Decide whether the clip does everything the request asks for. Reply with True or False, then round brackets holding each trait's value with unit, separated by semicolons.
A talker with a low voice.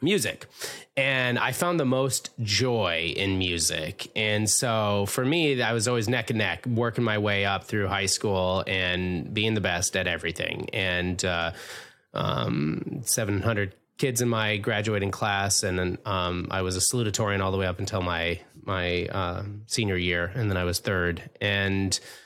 True (100 Hz)